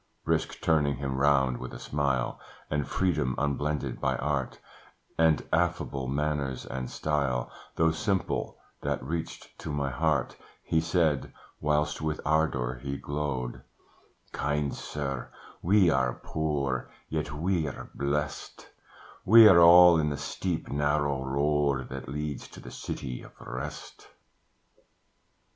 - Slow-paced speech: Yes, slow, 125 wpm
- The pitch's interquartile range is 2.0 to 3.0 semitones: Yes, narrow, 2.6 semitones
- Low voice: Yes, very low, 75 Hz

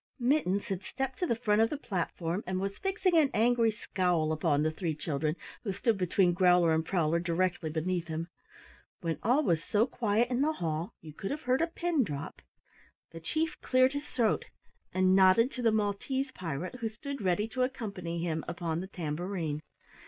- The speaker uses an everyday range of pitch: No, wide, 6.6 semitones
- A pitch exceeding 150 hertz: Yes, high, 190 Hz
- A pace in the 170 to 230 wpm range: Yes, average, 190 wpm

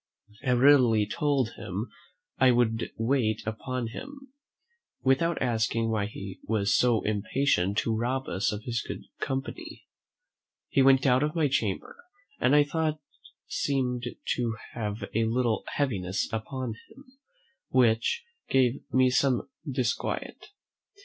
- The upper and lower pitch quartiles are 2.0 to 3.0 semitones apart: No, average, 3.4 semitones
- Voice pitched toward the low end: Yes, low, 125 Hz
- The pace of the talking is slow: Yes, slow, 130 wpm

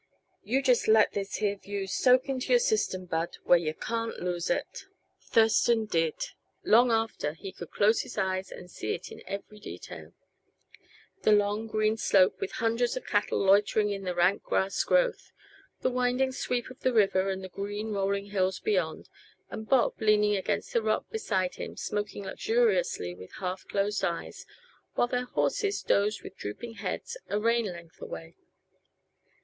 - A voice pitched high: Yes, high, 205 Hz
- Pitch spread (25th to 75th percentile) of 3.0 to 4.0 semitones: Yes, average, 3.6 semitones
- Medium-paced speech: Yes, average, 165 wpm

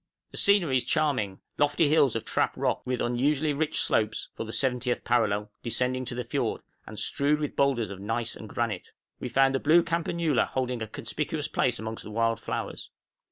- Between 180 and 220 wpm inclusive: Yes, average, 190 wpm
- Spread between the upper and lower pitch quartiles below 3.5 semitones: No, average, 4.4 semitones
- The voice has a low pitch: Yes, low, 125 Hz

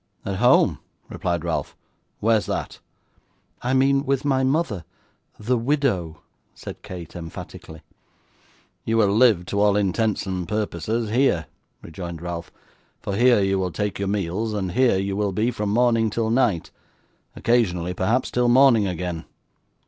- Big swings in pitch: No, average, 4.9 semitones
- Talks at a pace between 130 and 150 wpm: Yes, average, 145 wpm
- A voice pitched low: Yes, low, 105 Hz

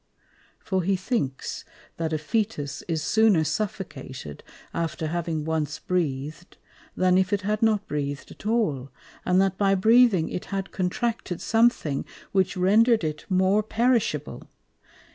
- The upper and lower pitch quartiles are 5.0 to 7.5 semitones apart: Yes, average, 5.3 semitones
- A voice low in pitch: No, medium, 185 Hz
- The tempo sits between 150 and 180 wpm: No, slow, 135 wpm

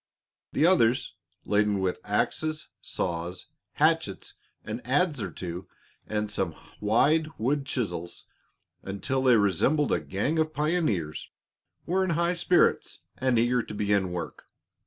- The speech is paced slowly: Yes, slow, 130 wpm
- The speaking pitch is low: Yes, low, 115 Hz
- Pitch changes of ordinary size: No, wide, 8.0 semitones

